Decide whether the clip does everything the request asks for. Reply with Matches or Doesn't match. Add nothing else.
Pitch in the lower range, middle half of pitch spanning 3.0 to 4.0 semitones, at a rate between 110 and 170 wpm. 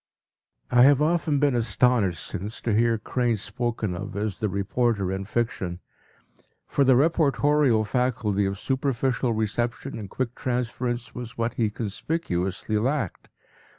Matches